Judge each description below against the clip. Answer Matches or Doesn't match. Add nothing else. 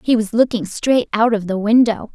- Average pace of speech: Doesn't match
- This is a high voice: Matches